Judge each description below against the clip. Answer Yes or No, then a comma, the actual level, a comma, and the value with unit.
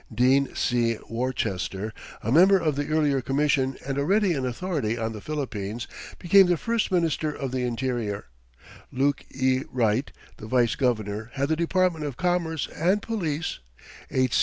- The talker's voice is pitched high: No, low, 135 Hz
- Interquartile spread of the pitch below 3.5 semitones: No, average, 5.2 semitones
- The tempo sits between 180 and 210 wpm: No, average, 155 wpm